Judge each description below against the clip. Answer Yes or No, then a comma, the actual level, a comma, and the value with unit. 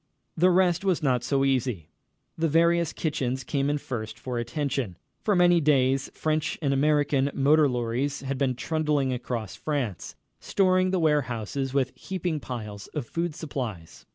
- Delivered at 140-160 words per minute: Yes, average, 155 wpm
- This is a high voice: No, medium, 140 Hz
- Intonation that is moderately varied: Yes, average, 4.0 semitones